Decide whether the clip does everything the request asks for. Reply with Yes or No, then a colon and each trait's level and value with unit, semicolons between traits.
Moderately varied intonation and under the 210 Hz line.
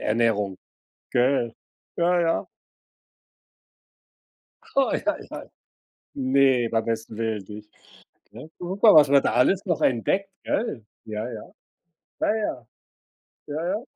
No: wide, 8.3 semitones; low, 135 Hz